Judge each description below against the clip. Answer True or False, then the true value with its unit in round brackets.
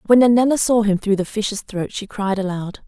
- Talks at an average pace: False (230 wpm)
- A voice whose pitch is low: False (210 Hz)